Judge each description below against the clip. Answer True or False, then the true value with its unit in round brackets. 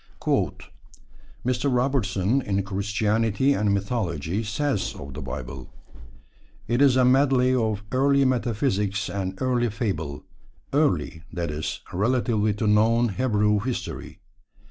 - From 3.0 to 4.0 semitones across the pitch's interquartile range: False (4.5 semitones)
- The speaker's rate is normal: False (115 wpm)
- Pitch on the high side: False (110 Hz)